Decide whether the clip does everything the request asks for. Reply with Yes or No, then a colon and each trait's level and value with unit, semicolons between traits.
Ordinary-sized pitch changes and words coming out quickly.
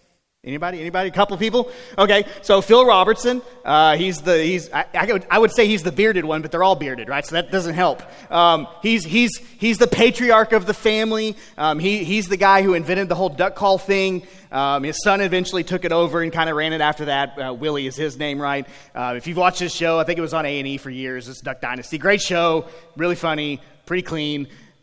Yes: average, 4.4 semitones; fast, 225 wpm